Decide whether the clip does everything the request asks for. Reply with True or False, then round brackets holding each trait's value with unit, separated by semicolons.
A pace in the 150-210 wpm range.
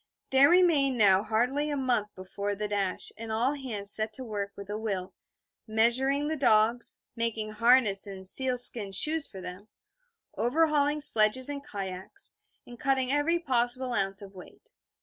True (160 wpm)